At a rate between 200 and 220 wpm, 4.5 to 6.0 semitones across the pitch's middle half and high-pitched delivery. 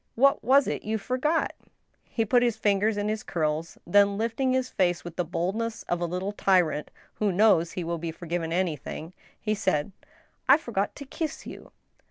Yes: fast, 205 wpm; average, 4.9 semitones; high, 200 Hz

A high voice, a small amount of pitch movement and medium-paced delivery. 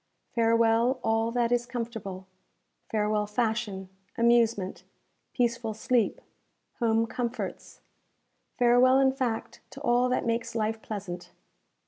No: high, 230 Hz; narrow, 1.8 semitones; slow, 105 wpm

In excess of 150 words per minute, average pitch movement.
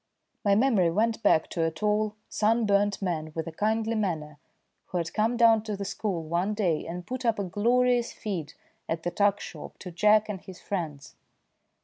Yes: average, 190 wpm; average, 4.2 semitones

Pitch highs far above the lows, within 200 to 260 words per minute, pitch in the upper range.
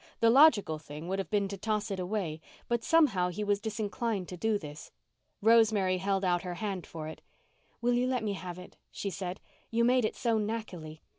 No: average, 3.8 semitones; fast, 205 wpm; high, 200 Hz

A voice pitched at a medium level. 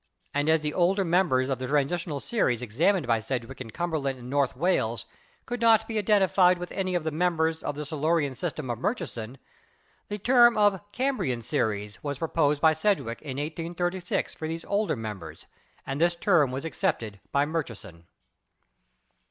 Yes: medium, 155 Hz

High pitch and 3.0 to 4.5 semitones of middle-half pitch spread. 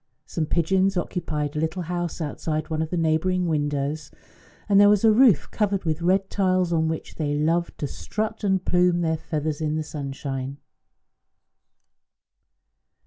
No: medium, 165 Hz; average, 3.3 semitones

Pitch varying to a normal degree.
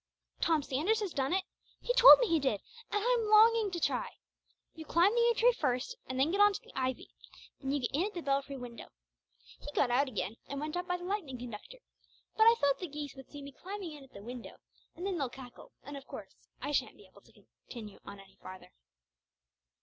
No: wide, 7.4 semitones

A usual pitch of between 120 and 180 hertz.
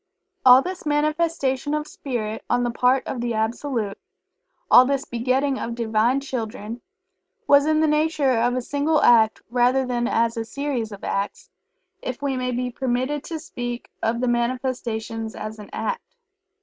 No: very high, 250 Hz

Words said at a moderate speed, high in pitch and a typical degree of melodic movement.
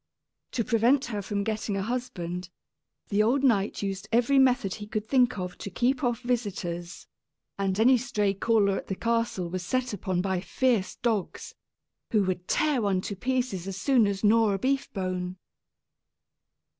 Yes: average, 170 wpm; high, 210 Hz; average, 4.4 semitones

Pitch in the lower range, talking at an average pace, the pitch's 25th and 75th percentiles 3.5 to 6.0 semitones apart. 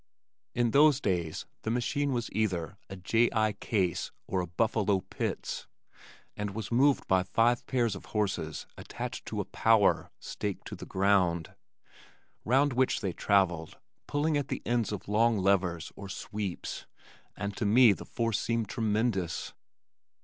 Yes: low, 105 Hz; average, 150 wpm; average, 3.8 semitones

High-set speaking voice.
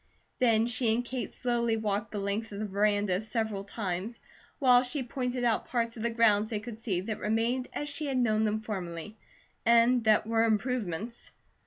Yes: high, 225 Hz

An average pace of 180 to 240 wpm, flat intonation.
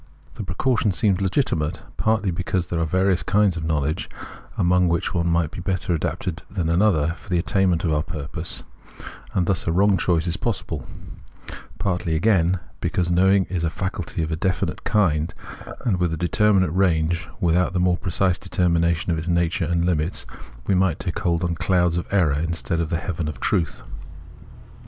Yes: average, 185 wpm; narrow, 2.3 semitones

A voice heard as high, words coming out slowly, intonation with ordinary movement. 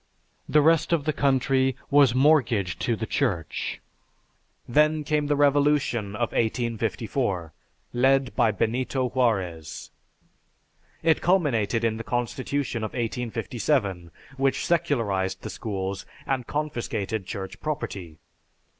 No: low, 120 Hz; slow, 110 wpm; average, 5.0 semitones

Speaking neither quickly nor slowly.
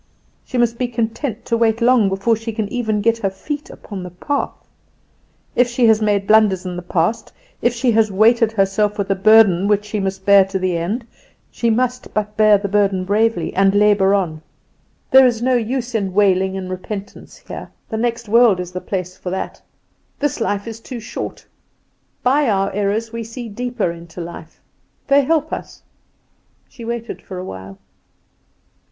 Yes: average, 185 wpm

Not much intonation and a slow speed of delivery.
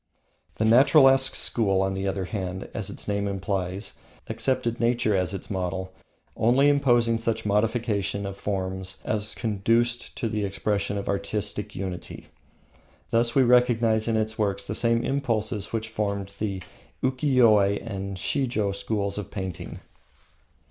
No: average, 3.1 semitones; slow, 130 wpm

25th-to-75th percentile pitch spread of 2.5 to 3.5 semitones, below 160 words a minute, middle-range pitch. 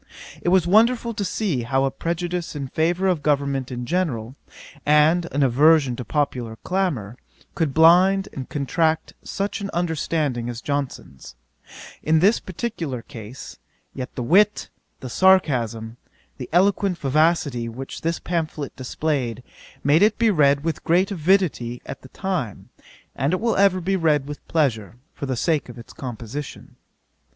No: wide, 5.6 semitones; average, 150 wpm; medium, 150 Hz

